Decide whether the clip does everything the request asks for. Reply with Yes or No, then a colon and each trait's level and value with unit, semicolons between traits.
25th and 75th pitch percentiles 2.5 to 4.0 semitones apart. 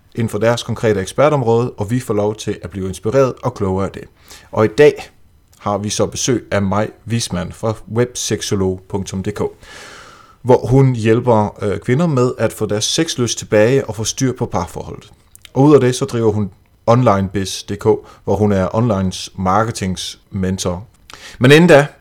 Yes: average, 3.4 semitones